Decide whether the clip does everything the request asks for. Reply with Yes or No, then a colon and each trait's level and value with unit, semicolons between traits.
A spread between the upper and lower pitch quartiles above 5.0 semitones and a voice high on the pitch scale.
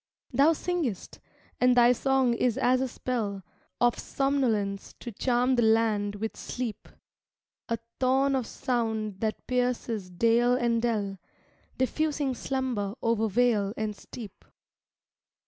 No: average, 3.0 semitones; high, 235 Hz